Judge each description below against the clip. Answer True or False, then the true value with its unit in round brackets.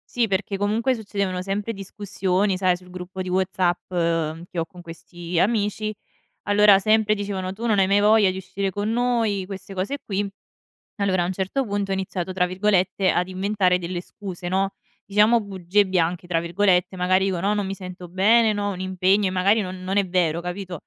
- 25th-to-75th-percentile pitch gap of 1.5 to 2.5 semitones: True (1.9 semitones)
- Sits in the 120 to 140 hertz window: False (190 Hz)